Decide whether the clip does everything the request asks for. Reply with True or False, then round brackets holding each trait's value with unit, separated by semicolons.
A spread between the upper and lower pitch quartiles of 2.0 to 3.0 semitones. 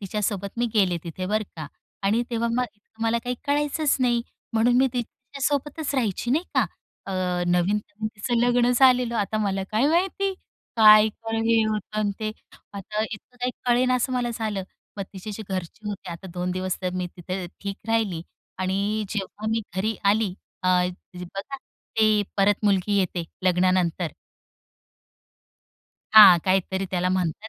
False (4.1 semitones)